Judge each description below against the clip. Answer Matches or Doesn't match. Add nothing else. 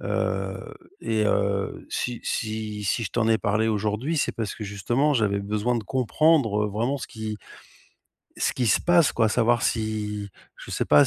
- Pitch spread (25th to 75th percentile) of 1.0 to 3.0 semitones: Matches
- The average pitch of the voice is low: Matches